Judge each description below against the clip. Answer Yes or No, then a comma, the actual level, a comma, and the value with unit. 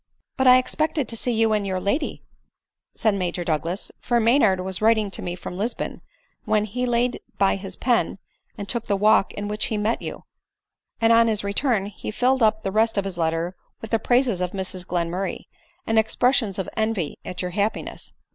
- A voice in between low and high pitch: No, high, 210 Hz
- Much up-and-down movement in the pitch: No, average, 3.4 semitones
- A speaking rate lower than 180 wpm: No, fast, 205 wpm